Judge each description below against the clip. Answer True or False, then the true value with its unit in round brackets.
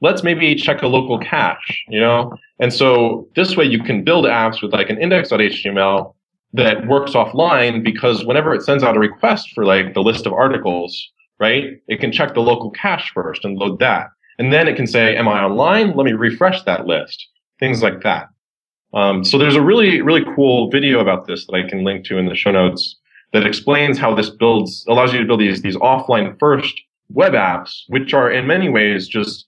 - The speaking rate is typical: False (210 wpm)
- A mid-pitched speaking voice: False (115 Hz)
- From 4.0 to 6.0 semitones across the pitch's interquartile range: True (5.0 semitones)